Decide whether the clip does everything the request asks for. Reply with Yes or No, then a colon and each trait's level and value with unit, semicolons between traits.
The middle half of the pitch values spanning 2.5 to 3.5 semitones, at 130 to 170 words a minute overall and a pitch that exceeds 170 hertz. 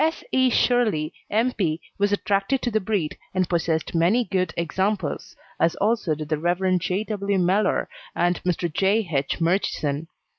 No: average, 4.1 semitones; average, 160 wpm; medium, 185 Hz